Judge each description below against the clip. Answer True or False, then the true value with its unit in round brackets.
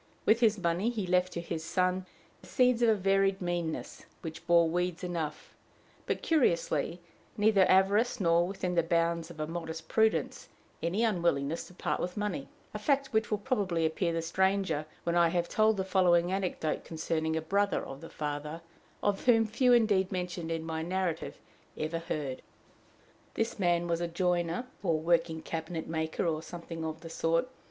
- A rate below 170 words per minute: False (175 wpm)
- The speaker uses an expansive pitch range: False (3.1 semitones)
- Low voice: False (175 Hz)